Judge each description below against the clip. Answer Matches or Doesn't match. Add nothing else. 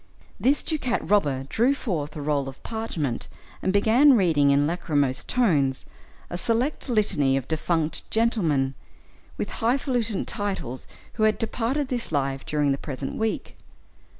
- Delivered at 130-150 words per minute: Matches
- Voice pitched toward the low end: Doesn't match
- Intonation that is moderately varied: Doesn't match